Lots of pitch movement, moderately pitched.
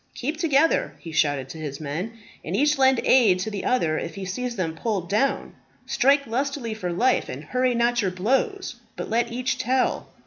No: wide, 6.4 semitones; high, 230 Hz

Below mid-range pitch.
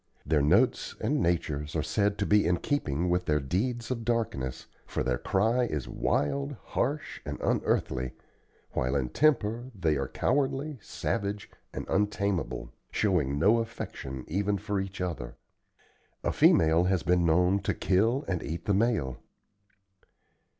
Yes: very low, 90 Hz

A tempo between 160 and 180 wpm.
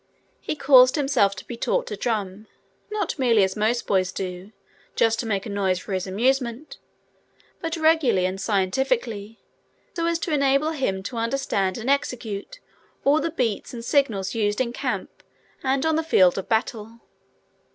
Yes: average, 165 wpm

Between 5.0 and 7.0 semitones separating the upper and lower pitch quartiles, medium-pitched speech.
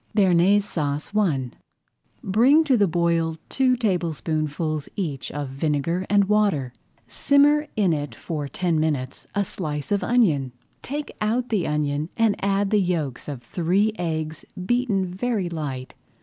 Yes: wide, 5.6 semitones; medium, 175 Hz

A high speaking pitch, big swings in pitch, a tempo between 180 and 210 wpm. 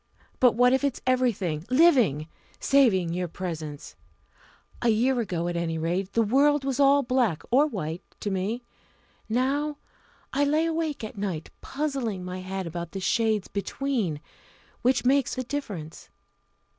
No: high, 225 Hz; wide, 7.0 semitones; average, 145 wpm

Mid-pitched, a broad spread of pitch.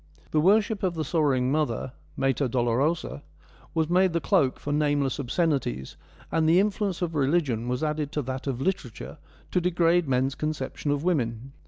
No: medium, 150 Hz; average, 4.5 semitones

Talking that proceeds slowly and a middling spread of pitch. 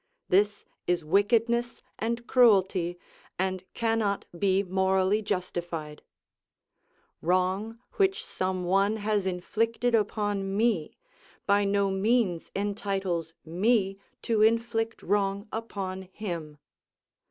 Yes: slow, 95 wpm; average, 3.0 semitones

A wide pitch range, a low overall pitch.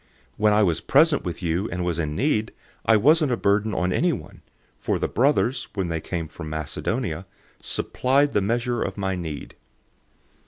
Yes: wide, 6.0 semitones; low, 100 Hz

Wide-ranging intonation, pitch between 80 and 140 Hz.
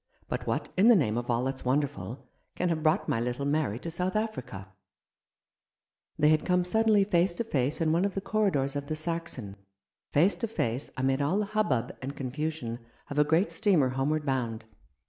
No: wide, 5.8 semitones; medium, 150 Hz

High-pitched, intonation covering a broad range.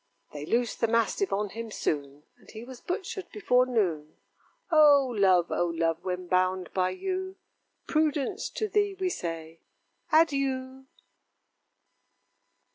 Yes: high, 230 Hz; wide, 8.9 semitones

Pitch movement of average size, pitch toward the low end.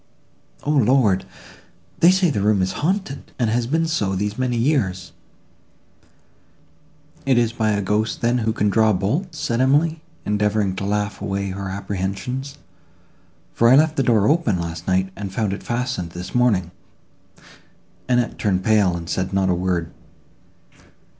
Yes: average, 5.0 semitones; low, 105 Hz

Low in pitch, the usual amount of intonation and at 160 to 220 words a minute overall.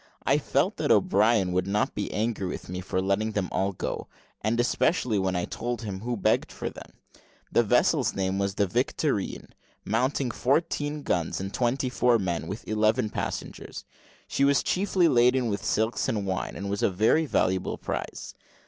Yes: low, 110 Hz; average, 4.2 semitones; average, 175 wpm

